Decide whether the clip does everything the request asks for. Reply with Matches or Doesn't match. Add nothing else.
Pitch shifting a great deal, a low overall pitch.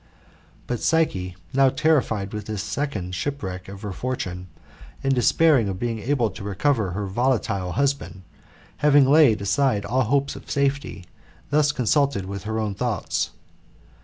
Matches